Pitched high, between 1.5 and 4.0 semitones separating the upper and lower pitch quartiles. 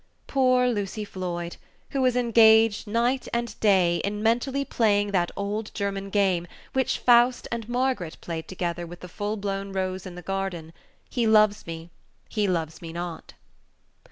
No: high, 200 Hz; average, 4.6 semitones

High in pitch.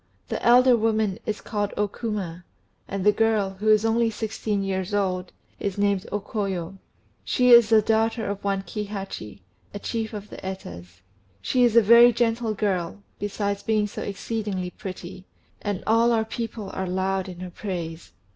Yes: high, 205 Hz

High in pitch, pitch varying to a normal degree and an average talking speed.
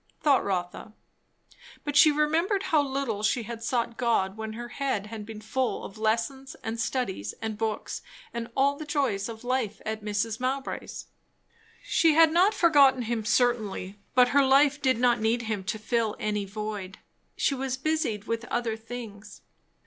Yes: high, 235 Hz; average, 3.9 semitones; average, 165 wpm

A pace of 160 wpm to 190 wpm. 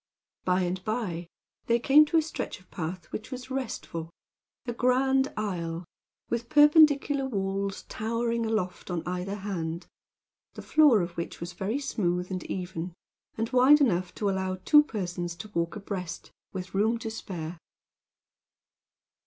No: average, 145 wpm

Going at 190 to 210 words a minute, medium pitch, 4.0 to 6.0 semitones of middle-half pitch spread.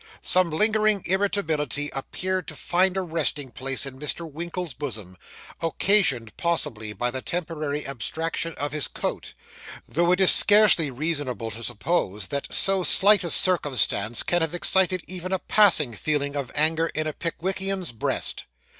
No: average, 150 wpm; medium, 160 Hz; average, 5.1 semitones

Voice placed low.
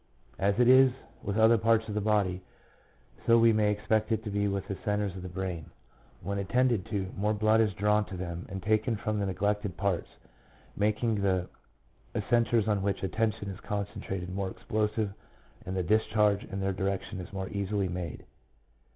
Yes: low, 100 Hz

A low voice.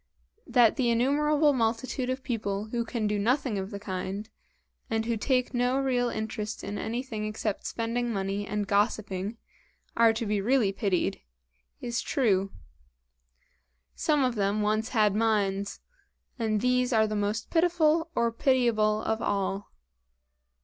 No: high, 225 Hz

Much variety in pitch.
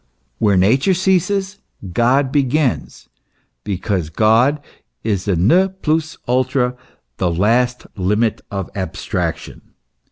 Yes: wide, 6.7 semitones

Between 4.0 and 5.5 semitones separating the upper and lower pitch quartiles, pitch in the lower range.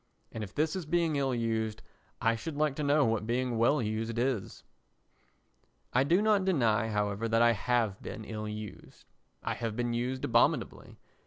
Yes: average, 4.3 semitones; low, 120 Hz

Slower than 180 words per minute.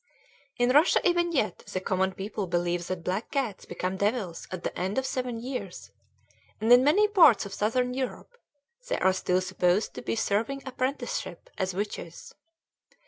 Yes: average, 165 wpm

